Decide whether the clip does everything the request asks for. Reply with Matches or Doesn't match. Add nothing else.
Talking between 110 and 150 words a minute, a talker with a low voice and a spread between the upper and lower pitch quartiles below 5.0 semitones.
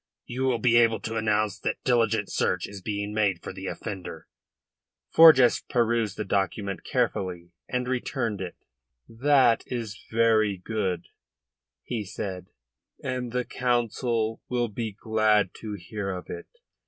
Matches